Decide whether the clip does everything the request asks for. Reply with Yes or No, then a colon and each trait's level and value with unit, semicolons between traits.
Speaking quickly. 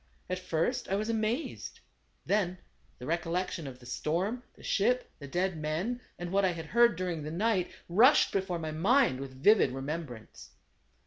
No: average, 170 wpm